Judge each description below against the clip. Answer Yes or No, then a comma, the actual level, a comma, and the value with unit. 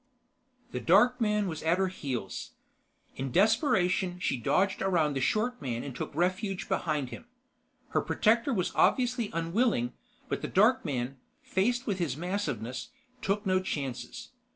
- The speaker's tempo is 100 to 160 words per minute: Yes, average, 150 wpm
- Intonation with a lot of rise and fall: Yes, wide, 6.6 semitones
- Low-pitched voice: No, medium, 185 Hz